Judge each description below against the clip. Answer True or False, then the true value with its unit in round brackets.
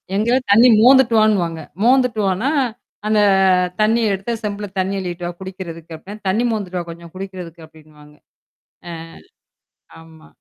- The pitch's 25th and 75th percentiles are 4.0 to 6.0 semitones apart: True (4.4 semitones)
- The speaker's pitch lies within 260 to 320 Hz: False (190 Hz)